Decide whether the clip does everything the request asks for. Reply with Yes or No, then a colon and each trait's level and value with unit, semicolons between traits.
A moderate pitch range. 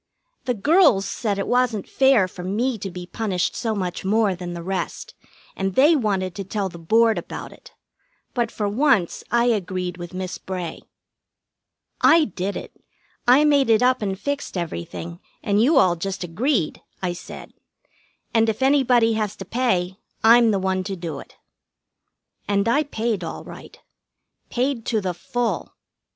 Yes: average, 4.6 semitones